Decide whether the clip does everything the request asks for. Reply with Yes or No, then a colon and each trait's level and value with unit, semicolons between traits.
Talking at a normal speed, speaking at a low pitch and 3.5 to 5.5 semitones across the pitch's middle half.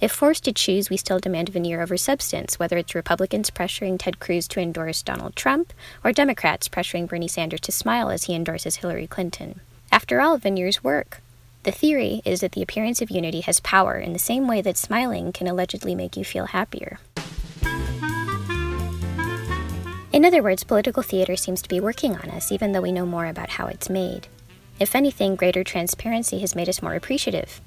No: average, 190 wpm; medium, 185 Hz; average, 4.1 semitones